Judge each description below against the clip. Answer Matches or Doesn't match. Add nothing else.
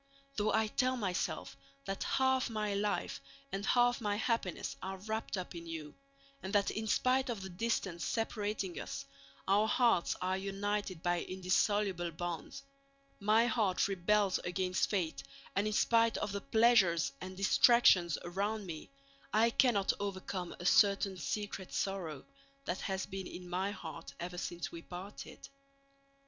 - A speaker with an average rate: Matches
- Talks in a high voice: Matches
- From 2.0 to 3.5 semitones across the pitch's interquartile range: Matches